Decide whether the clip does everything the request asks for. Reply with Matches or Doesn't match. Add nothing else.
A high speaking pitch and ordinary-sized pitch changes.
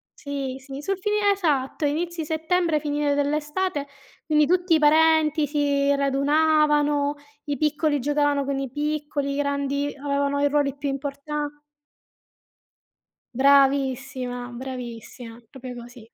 Doesn't match